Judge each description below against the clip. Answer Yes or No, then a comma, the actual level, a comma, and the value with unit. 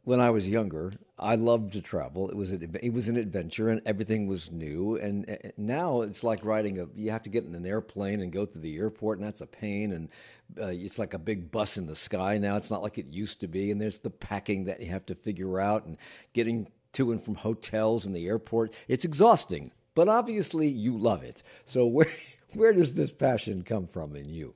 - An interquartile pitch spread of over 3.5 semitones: No, average, 3.1 semitones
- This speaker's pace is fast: Yes, fast, 230 wpm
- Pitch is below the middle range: Yes, low, 105 Hz